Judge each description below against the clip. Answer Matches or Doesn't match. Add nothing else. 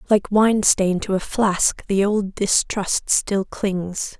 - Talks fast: Doesn't match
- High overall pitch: Matches